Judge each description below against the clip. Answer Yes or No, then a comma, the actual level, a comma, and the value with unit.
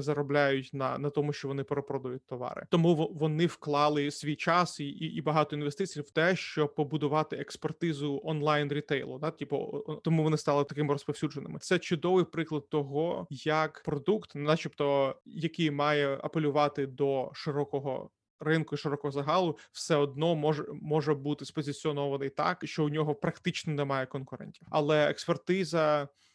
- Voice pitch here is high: No, medium, 150 Hz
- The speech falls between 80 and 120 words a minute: No, average, 140 wpm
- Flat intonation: Yes, narrow, 1.8 semitones